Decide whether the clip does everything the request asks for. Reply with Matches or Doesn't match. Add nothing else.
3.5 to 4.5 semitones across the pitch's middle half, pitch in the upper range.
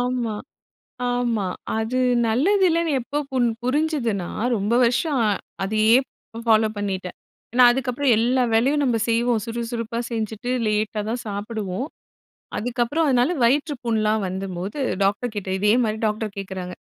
Doesn't match